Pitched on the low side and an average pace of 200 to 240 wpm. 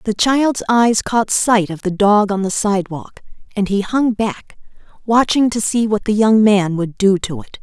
No: high, 210 Hz; fast, 205 wpm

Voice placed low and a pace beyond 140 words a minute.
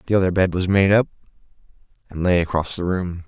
Yes: very low, 90 Hz; average, 200 wpm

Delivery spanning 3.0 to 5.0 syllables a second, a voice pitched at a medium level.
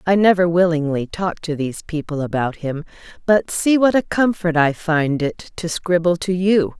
Yes: 4.7 syllables/s; medium, 170 Hz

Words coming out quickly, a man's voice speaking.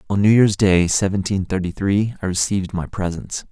No: average, 190 wpm; male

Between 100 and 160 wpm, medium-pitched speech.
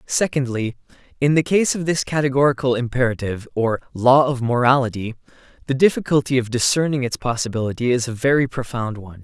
No: average, 150 wpm; low, 130 Hz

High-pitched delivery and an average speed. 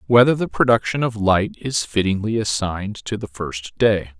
No: low, 105 Hz; average, 170 wpm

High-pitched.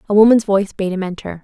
Yes: high, 200 Hz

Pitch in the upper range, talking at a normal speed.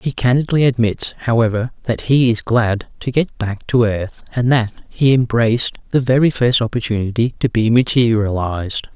No: low, 115 Hz; average, 160 wpm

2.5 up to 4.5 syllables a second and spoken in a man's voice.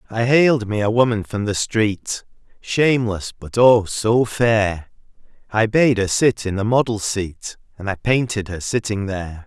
Yes: 4.2 syllables/s; male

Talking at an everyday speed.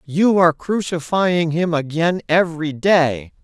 No: slow, 120 wpm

